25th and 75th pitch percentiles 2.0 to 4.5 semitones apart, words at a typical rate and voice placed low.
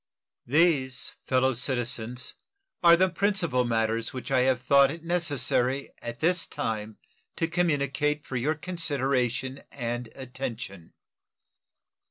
No: average, 4.2 semitones; slow, 115 wpm; low, 130 Hz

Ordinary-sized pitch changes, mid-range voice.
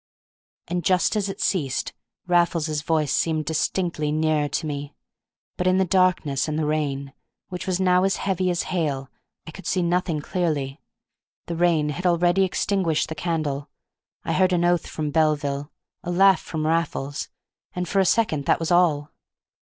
Yes: average, 3.2 semitones; medium, 165 Hz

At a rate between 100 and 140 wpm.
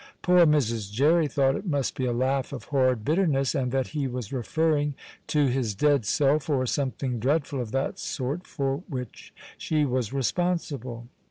No: average, 170 wpm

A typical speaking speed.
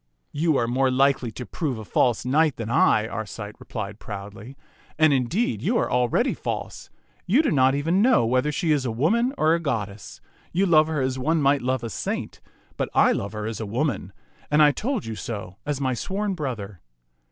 No: fast, 215 wpm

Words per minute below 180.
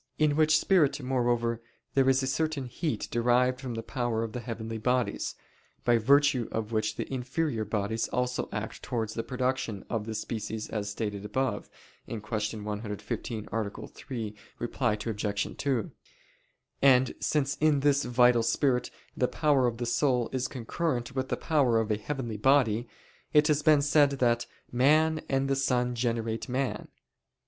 Yes: average, 155 wpm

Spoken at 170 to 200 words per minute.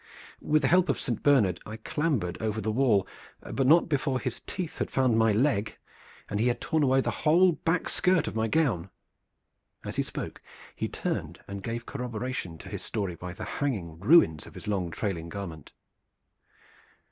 Yes: average, 180 wpm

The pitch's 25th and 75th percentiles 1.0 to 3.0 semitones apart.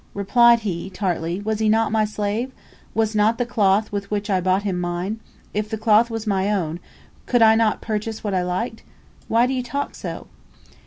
Yes: narrow, 2.6 semitones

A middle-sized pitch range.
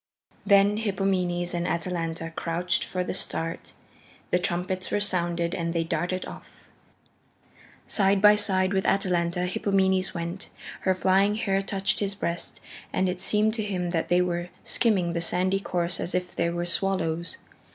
No: narrow, 2.1 semitones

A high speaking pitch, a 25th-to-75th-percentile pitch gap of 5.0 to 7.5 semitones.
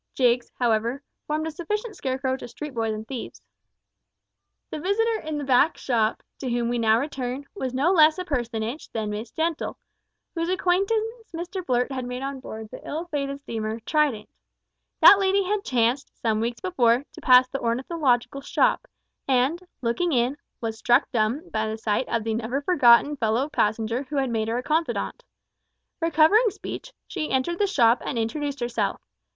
Yes: very high, 265 Hz; wide, 5.4 semitones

